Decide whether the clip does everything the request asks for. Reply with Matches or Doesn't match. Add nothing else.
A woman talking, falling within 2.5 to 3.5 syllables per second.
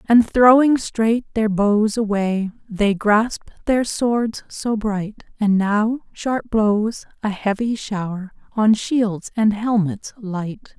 Matches